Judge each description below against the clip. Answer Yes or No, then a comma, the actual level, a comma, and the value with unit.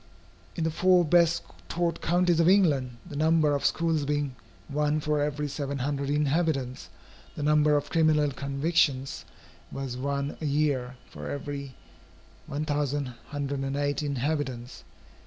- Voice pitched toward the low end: No, medium, 145 Hz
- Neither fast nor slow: No, slow, 125 wpm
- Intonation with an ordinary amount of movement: No, narrow, 2.0 semitones